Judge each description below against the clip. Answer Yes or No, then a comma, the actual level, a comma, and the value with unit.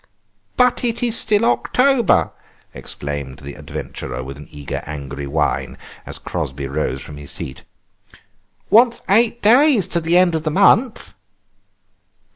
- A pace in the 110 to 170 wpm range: Yes, slow, 135 wpm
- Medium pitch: Yes, medium, 165 Hz